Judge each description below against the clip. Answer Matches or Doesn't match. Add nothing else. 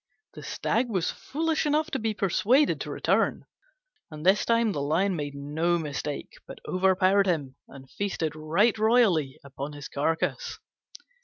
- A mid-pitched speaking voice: Matches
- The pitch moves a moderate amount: Doesn't match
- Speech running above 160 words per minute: Doesn't match